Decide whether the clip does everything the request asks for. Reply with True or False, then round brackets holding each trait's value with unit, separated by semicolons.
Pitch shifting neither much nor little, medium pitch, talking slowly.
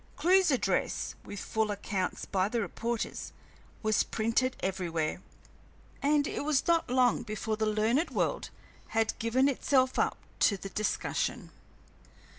False (3.9 semitones; 225 Hz; 130 wpm)